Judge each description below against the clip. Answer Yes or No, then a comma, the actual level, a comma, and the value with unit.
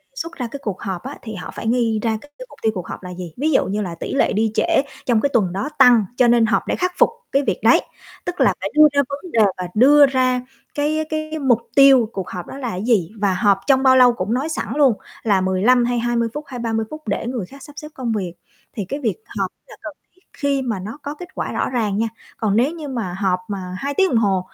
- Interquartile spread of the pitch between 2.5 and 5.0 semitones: No, wide, 5.4 semitones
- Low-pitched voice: No, high, 240 Hz